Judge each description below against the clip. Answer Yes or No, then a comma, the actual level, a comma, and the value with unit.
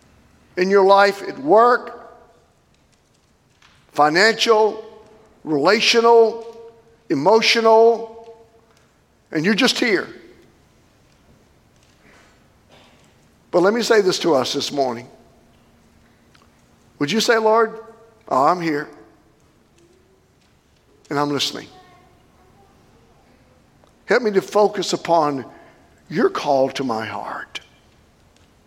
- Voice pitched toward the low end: No, high, 220 Hz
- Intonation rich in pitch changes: Yes, wide, 5.7 semitones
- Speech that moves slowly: Yes, slow, 85 wpm